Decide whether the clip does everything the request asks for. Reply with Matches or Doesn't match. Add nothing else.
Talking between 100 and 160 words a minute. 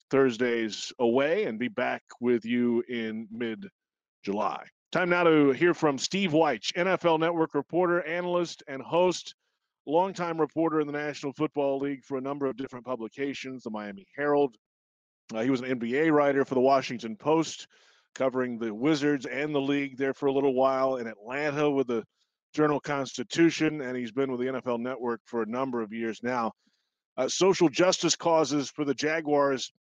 Doesn't match